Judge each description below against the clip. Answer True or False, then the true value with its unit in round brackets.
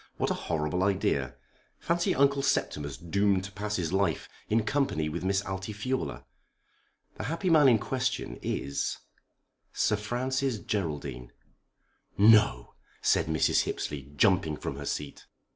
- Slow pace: True (130 wpm)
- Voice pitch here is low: True (100 Hz)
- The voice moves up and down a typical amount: False (7.9 semitones)